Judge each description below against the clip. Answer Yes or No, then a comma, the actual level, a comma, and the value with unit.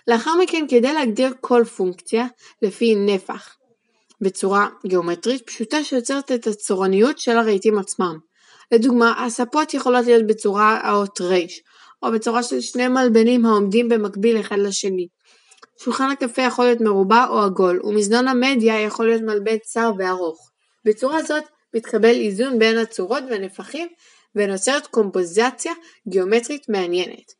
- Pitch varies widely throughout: No, average, 3.4 semitones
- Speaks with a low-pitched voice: No, high, 225 Hz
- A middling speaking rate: Yes, average, 125 wpm